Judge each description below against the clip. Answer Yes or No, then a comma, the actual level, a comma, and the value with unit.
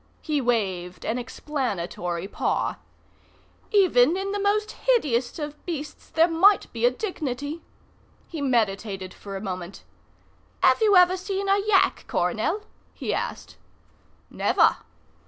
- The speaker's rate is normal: No, slow, 125 wpm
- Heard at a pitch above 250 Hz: Yes, very high, 290 Hz